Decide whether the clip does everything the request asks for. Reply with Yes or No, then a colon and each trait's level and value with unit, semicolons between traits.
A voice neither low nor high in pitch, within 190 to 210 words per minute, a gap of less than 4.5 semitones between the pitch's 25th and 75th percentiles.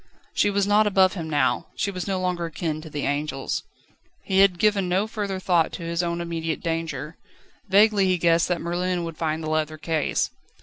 Yes: medium, 170 Hz; average, 200 wpm; average, 3.1 semitones